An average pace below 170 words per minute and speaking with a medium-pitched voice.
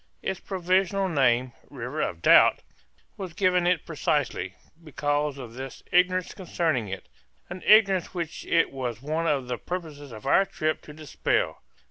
Yes: average, 150 wpm; medium, 155 Hz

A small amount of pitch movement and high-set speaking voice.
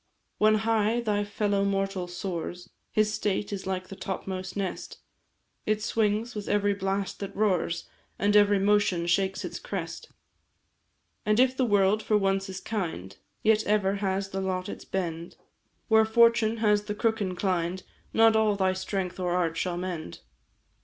Yes: narrow, 2.3 semitones; high, 200 Hz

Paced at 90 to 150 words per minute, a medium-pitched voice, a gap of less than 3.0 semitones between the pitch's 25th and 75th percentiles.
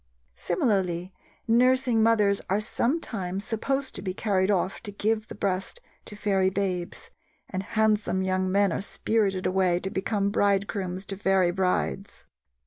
No: average, 140 wpm; high, 195 Hz; narrow, 2.5 semitones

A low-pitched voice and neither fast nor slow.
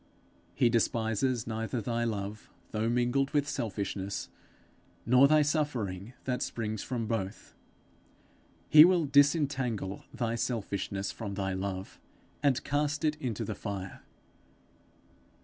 No: low, 115 Hz; slow, 115 wpm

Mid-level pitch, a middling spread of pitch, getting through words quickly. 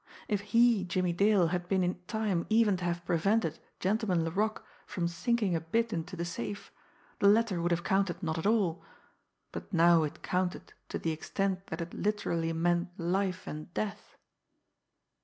No: medium, 180 Hz; average, 3.3 semitones; average, 170 wpm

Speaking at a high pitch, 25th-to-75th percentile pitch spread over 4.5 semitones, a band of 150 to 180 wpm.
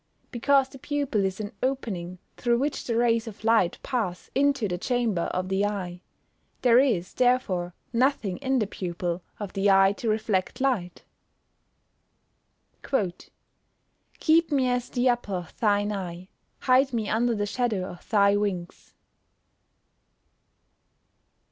No: high, 215 Hz; average, 5.0 semitones; average, 140 wpm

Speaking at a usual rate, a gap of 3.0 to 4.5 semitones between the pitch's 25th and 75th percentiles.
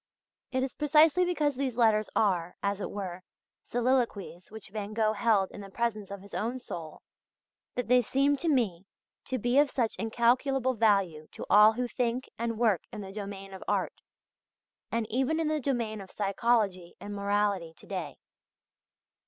Yes: average, 170 wpm; average, 4.0 semitones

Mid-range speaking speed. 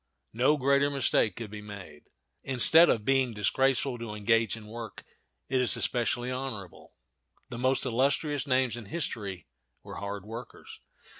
Yes: average, 145 wpm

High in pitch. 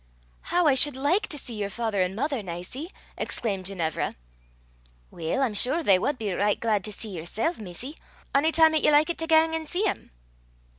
Yes: very high, 250 Hz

